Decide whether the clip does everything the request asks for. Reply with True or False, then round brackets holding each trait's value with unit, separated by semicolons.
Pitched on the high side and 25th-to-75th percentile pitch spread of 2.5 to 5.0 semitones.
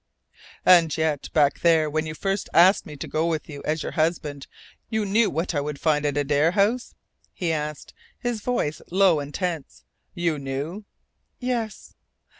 False (160 Hz; 4.5 semitones)